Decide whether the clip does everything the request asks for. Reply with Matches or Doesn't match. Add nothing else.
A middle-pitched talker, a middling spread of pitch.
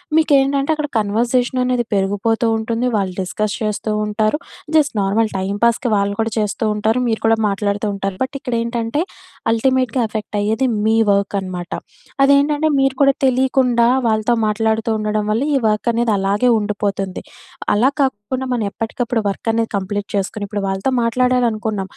Doesn't match